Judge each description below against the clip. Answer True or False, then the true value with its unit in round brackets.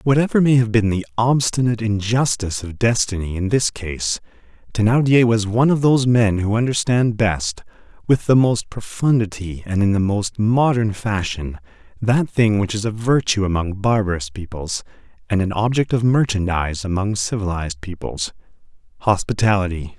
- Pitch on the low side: True (105 Hz)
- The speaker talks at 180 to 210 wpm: False (145 wpm)